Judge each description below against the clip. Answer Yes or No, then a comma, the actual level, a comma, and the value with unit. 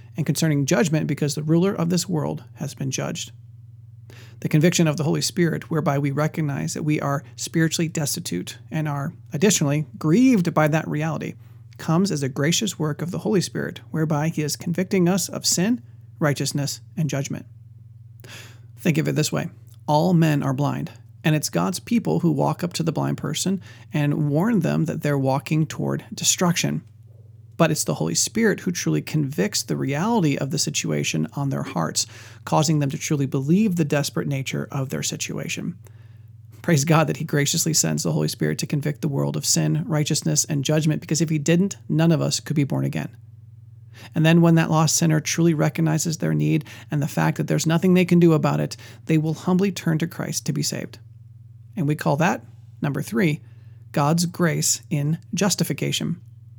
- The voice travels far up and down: Yes, wide, 6.0 semitones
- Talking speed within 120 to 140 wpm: No, average, 185 wpm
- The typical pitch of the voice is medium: Yes, medium, 150 Hz